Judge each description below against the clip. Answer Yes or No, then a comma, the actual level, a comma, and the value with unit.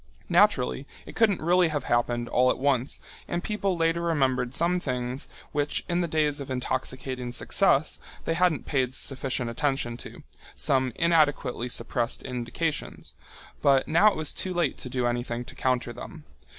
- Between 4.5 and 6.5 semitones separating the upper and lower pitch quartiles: Yes, average, 4.8 semitones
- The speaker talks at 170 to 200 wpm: No, average, 160 wpm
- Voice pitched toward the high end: No, low, 135 Hz